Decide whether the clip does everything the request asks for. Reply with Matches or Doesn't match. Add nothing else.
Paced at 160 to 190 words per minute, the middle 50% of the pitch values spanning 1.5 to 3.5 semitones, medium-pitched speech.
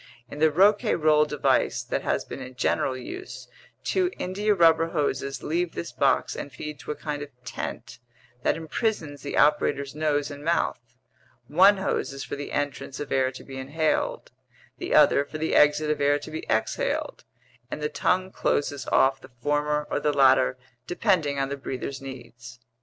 Matches